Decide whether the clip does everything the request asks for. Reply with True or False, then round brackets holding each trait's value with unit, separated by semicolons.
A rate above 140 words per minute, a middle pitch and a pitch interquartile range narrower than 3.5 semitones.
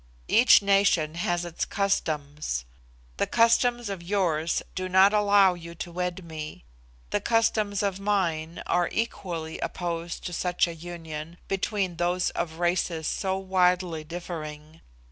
False (135 wpm; 175 Hz; 3.1 semitones)